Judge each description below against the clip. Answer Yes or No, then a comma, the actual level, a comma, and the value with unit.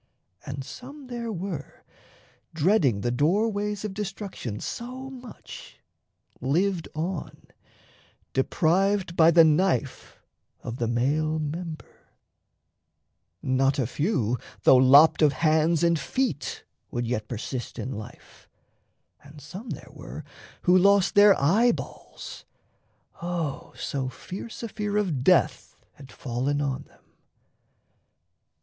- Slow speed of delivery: Yes, slow, 115 wpm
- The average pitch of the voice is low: No, medium, 160 Hz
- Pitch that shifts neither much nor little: No, wide, 6.9 semitones